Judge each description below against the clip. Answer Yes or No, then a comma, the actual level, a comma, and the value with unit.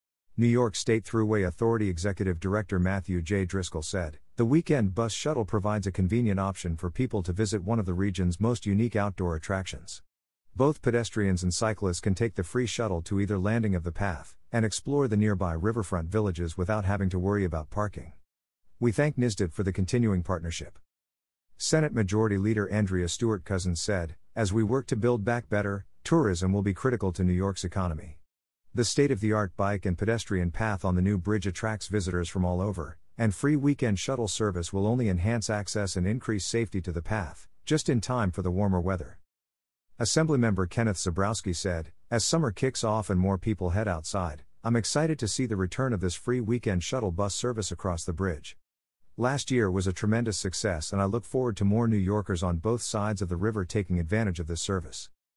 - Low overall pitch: Yes, low, 100 Hz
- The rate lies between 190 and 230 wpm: Yes, average, 195 wpm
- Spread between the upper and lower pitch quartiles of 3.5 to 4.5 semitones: Yes, average, 3.8 semitones